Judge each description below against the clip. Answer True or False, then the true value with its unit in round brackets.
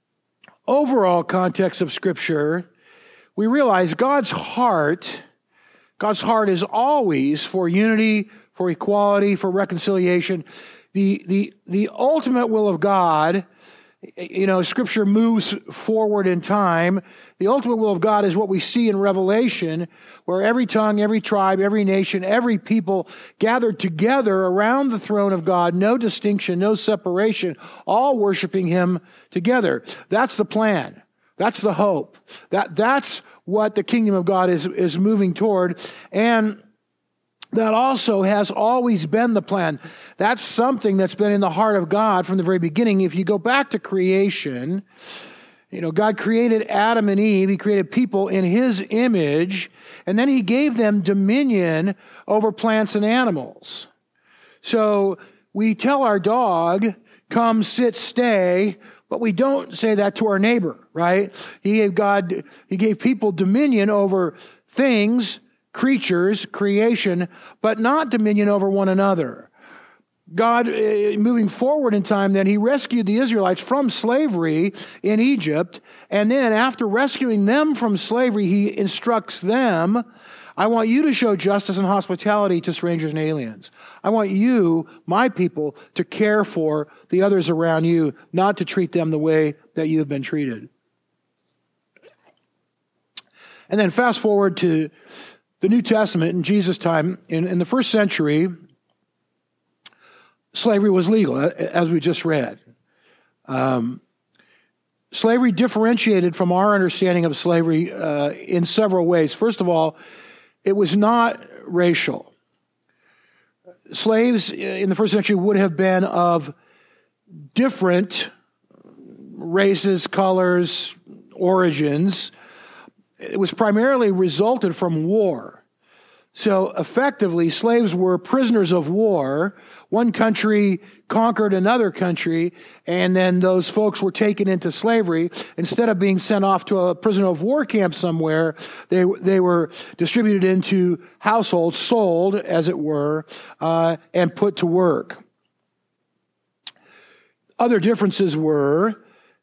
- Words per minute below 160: True (135 wpm)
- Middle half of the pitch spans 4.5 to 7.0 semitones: False (3.7 semitones)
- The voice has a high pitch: True (200 Hz)